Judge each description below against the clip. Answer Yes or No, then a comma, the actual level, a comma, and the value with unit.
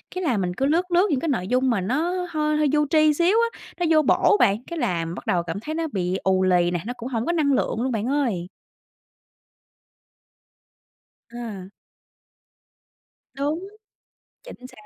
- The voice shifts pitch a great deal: Yes, wide, 8.1 semitones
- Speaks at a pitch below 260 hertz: No, very high, 265 Hz